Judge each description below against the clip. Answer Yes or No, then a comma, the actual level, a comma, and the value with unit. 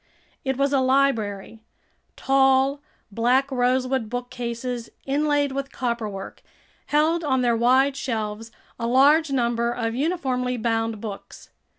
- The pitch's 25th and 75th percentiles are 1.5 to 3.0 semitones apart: Yes, average, 2.7 semitones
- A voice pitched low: No, very high, 255 Hz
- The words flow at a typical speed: No, slow, 115 wpm